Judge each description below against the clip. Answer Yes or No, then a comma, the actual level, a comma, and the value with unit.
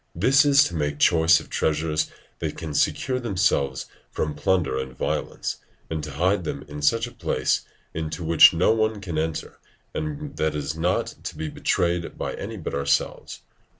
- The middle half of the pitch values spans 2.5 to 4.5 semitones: Yes, average, 4.2 semitones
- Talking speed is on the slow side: No, average, 180 wpm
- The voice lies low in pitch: Yes, very low, 80 Hz